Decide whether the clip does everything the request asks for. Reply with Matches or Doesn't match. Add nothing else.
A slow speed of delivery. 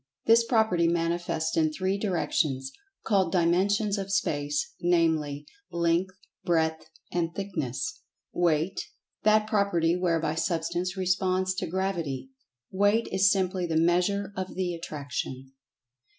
Matches